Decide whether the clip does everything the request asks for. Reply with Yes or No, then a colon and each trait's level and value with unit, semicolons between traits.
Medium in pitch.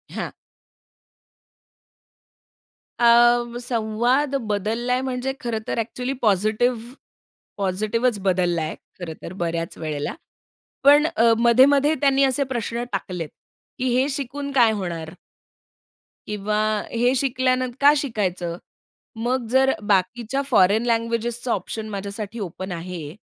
No: high, 230 Hz